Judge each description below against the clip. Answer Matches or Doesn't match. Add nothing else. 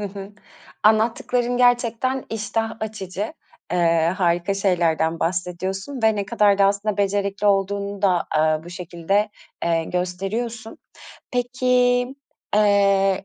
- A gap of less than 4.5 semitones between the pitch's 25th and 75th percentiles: Matches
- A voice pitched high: Matches